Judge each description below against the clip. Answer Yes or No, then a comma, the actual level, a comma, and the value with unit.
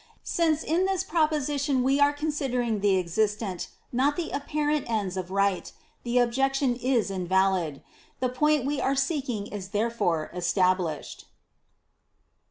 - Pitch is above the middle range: Yes, high, 245 Hz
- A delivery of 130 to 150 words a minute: Yes, average, 140 wpm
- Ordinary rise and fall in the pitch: No, wide, 6.8 semitones